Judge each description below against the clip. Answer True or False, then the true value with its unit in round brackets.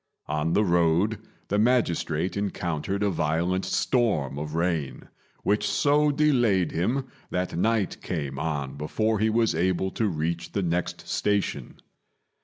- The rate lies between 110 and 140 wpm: True (135 wpm)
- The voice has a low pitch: True (90 Hz)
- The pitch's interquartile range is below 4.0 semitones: False (4.8 semitones)